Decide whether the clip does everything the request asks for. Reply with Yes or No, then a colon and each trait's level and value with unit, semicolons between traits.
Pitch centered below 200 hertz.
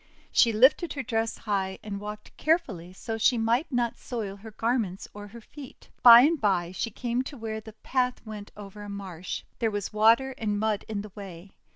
No: high, 220 Hz